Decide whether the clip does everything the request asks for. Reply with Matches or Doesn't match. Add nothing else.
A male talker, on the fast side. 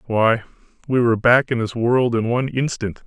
Doesn't match